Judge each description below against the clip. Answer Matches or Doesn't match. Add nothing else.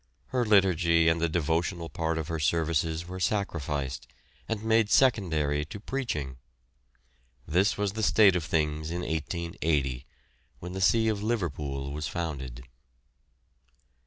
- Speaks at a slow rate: Matches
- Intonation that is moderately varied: Matches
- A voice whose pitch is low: Matches